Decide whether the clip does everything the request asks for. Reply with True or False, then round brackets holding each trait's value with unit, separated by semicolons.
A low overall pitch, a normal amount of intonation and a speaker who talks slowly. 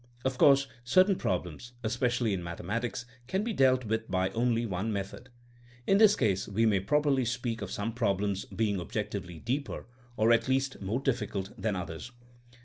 False (115 Hz; 4.5 semitones; 165 wpm)